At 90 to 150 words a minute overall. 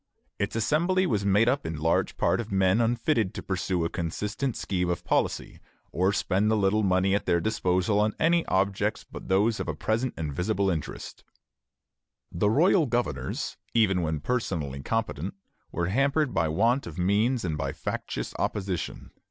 No: average, 165 wpm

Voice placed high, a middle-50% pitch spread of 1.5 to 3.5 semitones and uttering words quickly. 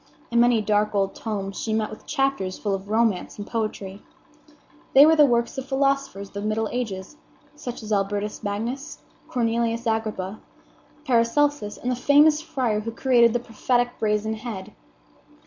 No: high, 225 Hz; average, 3.2 semitones; average, 160 wpm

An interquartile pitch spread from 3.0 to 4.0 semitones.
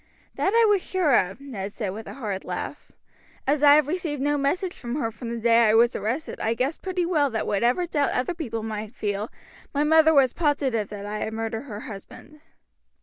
No: wide, 5.5 semitones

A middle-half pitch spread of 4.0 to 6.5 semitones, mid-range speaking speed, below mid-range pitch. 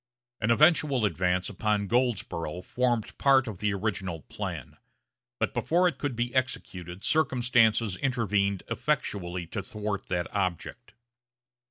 No: average, 5.1 semitones; slow, 125 wpm; low, 105 Hz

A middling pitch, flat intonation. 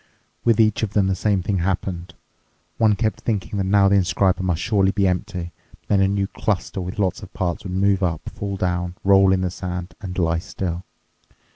No: very low, 95 Hz; narrow, 1.8 semitones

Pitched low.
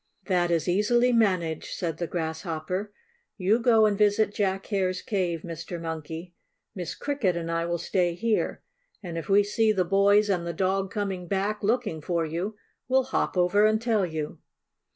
No: high, 190 Hz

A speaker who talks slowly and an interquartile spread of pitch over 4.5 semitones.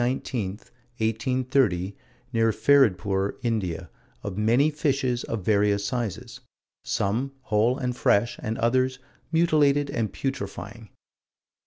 No: slow, 105 wpm; average, 4.0 semitones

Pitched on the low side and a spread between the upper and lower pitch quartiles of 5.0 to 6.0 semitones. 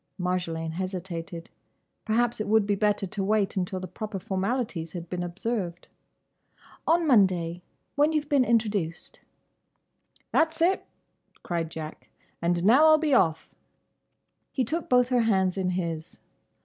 No: high, 195 Hz; wide, 5.6 semitones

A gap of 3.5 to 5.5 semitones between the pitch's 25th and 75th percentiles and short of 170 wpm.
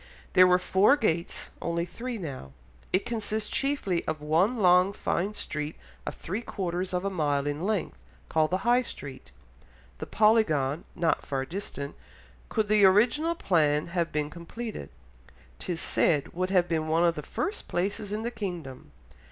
Yes: average, 5.0 semitones; average, 160 wpm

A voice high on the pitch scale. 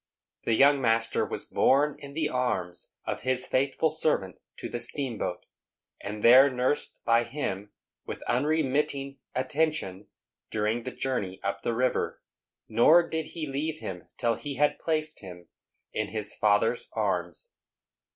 No: low, 125 Hz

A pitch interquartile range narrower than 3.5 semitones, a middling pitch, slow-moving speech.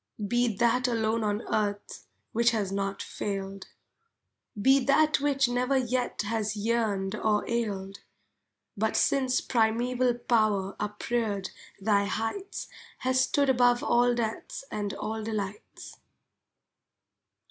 No: average, 3.1 semitones; high, 225 Hz; slow, 115 wpm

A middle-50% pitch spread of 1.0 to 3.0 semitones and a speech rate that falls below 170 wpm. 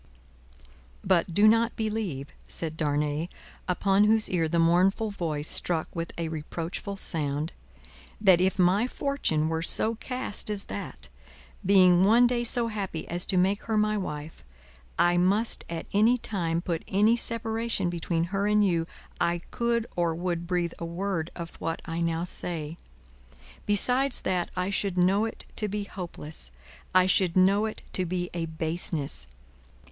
No: average, 4.0 semitones; average, 155 wpm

